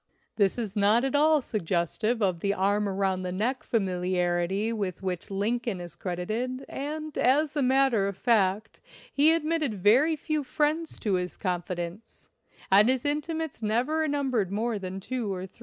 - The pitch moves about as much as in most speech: No, wide, 6.1 semitones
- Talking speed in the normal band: Yes, average, 165 wpm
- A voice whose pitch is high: Yes, high, 215 Hz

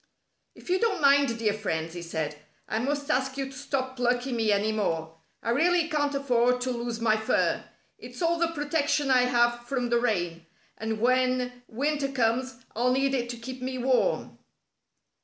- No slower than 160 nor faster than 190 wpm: Yes, average, 180 wpm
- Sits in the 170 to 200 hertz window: No, very high, 250 Hz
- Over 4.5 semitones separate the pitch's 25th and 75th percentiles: No, average, 3.3 semitones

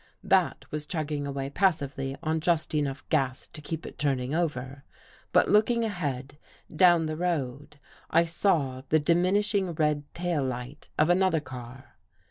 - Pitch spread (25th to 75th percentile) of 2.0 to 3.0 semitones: No, average, 4.0 semitones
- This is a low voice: No, medium, 150 Hz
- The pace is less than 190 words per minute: Yes, average, 150 wpm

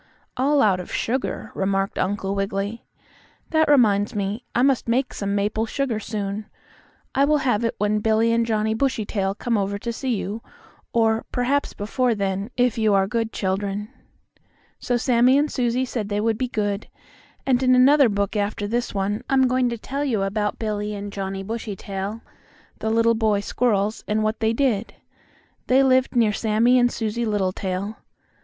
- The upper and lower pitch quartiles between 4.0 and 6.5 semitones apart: No, average, 3.3 semitones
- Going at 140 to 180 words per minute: Yes, average, 170 wpm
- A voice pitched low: No, high, 220 Hz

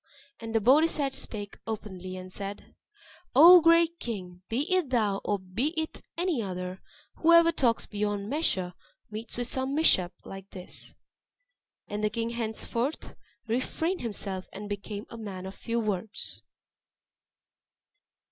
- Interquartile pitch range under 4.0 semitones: No, wide, 5.6 semitones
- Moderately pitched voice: No, high, 220 Hz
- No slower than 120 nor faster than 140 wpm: Yes, slow, 135 wpm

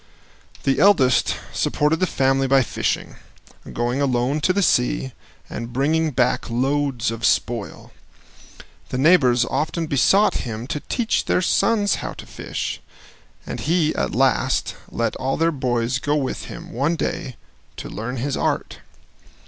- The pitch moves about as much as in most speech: Yes, average, 4.3 semitones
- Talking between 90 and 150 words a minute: Yes, average, 145 wpm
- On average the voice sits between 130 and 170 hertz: Yes, low, 135 Hz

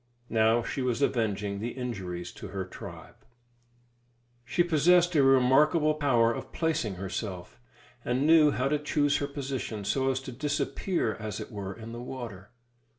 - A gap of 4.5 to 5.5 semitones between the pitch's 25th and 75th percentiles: Yes, average, 5.1 semitones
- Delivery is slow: No, average, 155 wpm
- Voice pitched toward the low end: Yes, low, 125 Hz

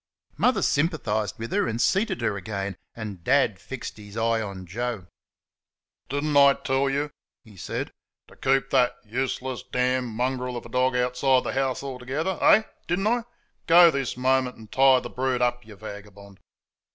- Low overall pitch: Yes, low, 125 Hz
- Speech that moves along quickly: No, average, 175 wpm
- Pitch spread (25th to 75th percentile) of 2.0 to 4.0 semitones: Yes, average, 3.6 semitones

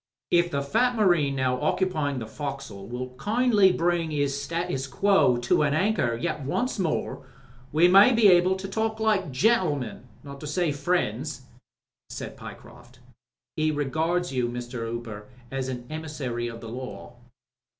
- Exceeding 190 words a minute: No, average, 155 wpm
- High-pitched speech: No, medium, 150 Hz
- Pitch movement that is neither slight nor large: No, wide, 6.0 semitones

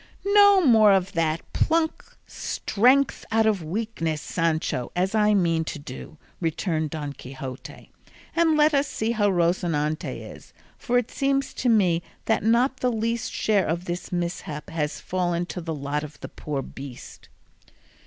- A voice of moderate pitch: Yes, medium, 180 Hz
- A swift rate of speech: No, average, 155 wpm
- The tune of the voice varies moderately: No, wide, 6.6 semitones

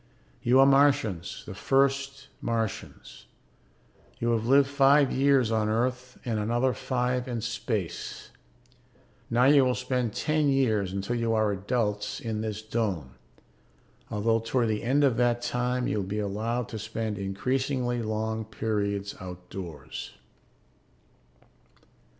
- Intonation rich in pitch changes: No, average, 3.3 semitones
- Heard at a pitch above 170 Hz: No, low, 115 Hz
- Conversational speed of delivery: No, slow, 130 wpm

